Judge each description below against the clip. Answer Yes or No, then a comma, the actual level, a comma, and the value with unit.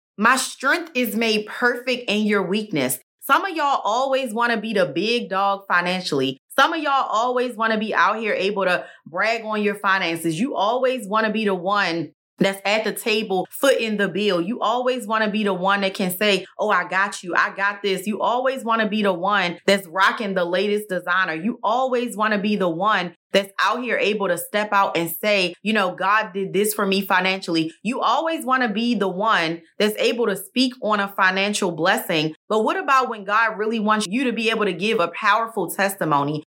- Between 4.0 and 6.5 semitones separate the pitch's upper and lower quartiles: No, average, 3.5 semitones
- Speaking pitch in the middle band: No, high, 205 Hz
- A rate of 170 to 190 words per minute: No, fast, 205 wpm